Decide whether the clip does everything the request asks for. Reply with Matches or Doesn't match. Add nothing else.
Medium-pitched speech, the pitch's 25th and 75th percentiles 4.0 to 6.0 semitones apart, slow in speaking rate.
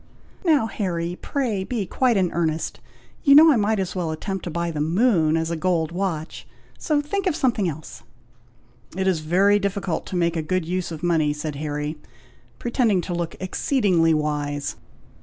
Doesn't match